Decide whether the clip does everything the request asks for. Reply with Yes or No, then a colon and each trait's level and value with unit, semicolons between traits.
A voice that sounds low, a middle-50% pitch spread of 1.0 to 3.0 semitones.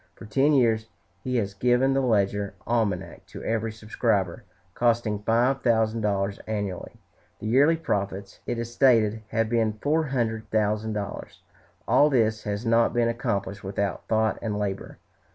Yes: low, 110 Hz; narrow, 2.5 semitones